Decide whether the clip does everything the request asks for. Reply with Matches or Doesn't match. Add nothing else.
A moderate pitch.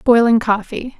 Doesn't match